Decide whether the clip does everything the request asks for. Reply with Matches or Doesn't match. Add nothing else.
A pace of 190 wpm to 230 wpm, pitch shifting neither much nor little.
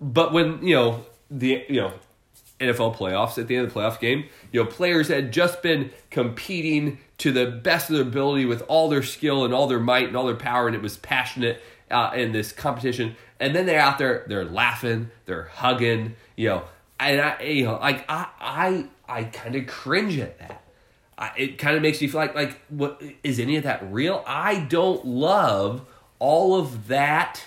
Matches